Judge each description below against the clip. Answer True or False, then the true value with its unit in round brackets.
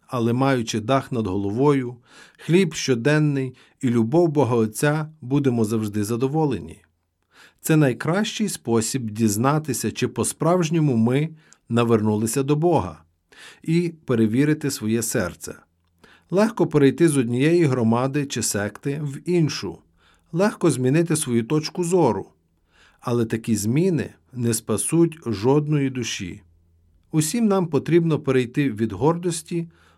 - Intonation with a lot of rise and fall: True (5.8 semitones)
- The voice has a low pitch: True (130 Hz)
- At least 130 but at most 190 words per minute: False (110 wpm)